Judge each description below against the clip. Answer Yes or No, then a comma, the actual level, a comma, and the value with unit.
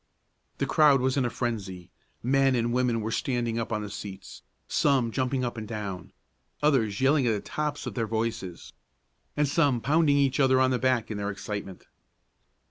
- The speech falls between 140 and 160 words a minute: No, average, 185 wpm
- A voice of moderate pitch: No, low, 120 Hz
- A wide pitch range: No, average, 3.9 semitones